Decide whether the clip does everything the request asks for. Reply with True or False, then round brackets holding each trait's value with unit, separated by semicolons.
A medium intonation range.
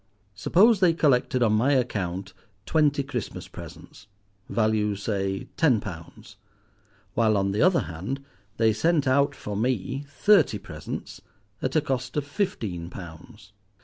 False (6.0 semitones)